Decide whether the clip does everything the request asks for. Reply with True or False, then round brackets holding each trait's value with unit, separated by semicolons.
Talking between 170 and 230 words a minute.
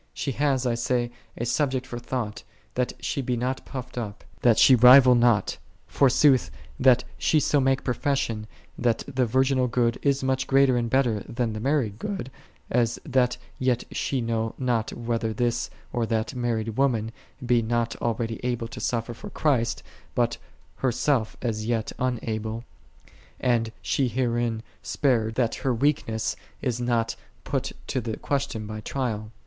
False (155 wpm)